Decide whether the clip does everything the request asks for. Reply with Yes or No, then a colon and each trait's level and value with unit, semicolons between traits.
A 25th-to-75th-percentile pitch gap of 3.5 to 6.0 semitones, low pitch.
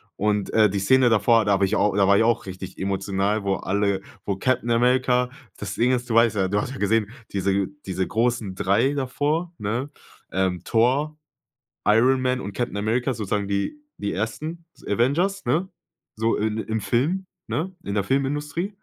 Yes: average, 4.4 semitones; low, 115 Hz